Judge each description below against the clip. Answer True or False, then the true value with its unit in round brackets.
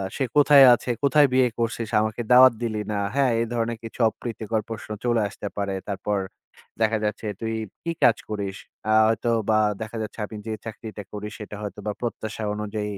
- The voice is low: True (110 Hz)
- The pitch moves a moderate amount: False (2.0 semitones)